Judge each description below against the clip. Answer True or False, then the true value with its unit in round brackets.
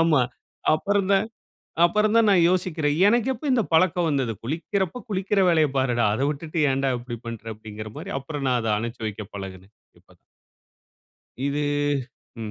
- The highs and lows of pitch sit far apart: True (8.1 semitones)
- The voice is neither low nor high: True (150 Hz)